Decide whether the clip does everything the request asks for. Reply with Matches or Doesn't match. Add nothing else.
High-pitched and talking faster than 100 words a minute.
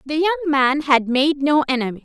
Matches